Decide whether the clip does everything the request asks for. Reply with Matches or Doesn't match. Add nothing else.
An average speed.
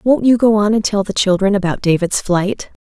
Doesn't match